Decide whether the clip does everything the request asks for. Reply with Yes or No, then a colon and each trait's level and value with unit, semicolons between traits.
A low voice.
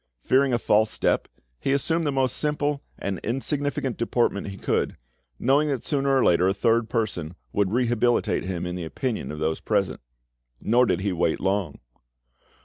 Yes: low, 115 Hz